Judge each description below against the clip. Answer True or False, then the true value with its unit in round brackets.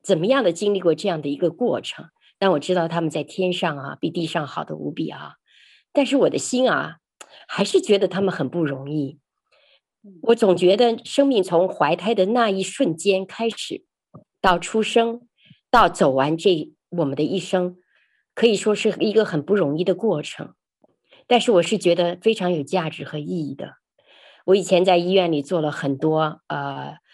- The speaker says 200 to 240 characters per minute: False (255 characters per minute)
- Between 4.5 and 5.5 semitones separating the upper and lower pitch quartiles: True (4.9 semitones)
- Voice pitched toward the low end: False (185 Hz)